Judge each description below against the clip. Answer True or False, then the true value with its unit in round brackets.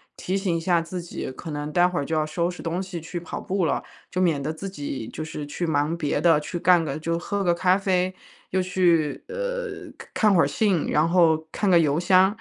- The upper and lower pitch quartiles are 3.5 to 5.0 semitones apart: False (2.9 semitones)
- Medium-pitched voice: True (175 Hz)